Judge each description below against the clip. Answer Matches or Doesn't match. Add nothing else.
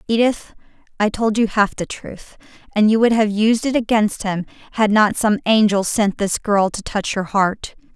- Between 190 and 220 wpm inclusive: Matches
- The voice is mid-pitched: Doesn't match